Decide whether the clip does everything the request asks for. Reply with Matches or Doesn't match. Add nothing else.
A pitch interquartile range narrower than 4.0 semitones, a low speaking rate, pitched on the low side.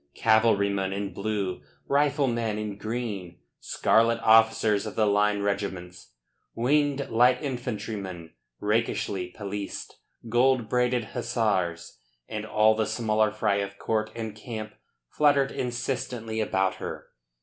Matches